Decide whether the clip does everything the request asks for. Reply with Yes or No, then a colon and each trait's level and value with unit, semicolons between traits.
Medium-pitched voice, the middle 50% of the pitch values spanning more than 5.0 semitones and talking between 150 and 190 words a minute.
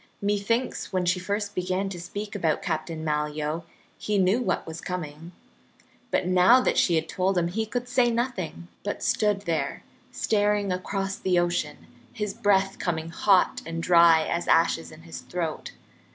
No: medium, 180 Hz; average, 3.6 semitones; average, 165 wpm